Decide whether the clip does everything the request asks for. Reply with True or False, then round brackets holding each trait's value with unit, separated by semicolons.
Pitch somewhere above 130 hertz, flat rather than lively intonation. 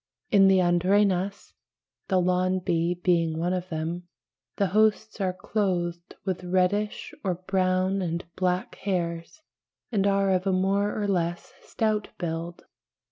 True (185 Hz; 2.1 semitones)